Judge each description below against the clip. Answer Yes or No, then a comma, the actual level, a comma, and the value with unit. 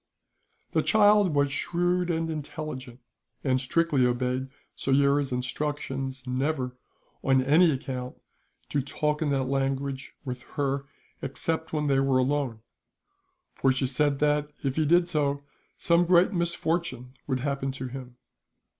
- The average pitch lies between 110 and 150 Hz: Yes, medium, 140 Hz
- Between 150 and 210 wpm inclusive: No, slow, 135 wpm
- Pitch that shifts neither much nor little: Yes, average, 3.0 semitones